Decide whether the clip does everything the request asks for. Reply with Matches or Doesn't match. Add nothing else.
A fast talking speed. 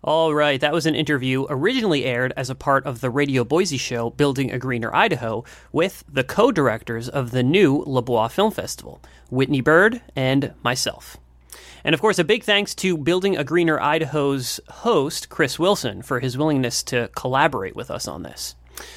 Doesn't match